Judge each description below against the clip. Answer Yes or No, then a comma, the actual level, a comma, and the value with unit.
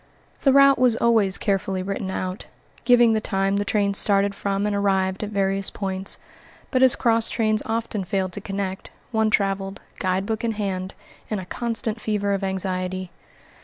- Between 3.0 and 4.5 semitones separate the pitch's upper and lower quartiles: No, narrow, 2.4 semitones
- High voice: Yes, high, 200 Hz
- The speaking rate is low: No, average, 165 wpm